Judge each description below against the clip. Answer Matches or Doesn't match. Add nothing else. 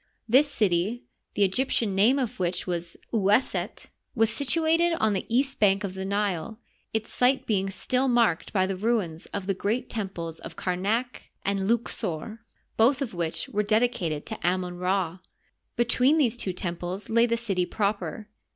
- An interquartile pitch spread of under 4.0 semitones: Doesn't match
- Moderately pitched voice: Doesn't match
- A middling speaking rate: Matches